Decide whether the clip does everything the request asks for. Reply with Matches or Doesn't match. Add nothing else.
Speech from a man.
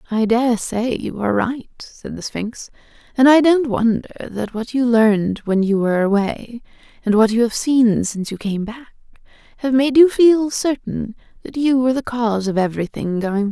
Doesn't match